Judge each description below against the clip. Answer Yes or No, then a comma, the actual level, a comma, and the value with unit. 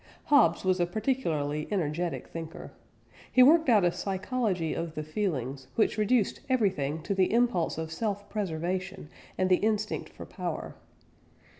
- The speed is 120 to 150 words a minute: Yes, average, 145 wpm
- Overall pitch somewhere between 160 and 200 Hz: Yes, medium, 185 Hz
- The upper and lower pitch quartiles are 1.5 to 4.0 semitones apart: No, average, 4.9 semitones